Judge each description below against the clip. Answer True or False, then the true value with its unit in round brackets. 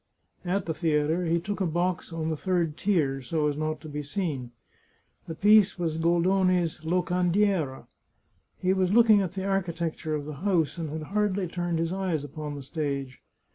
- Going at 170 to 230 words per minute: True (180 wpm)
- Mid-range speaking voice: True (170 Hz)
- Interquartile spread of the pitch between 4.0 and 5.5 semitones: False (3.3 semitones)